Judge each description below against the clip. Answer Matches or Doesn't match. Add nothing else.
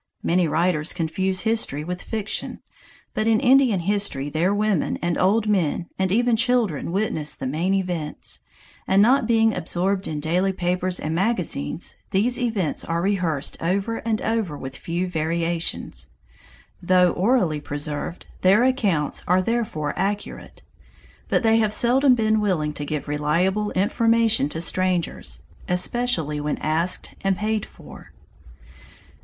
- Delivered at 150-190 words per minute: Doesn't match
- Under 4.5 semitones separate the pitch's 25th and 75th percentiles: Doesn't match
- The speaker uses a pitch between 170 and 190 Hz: Matches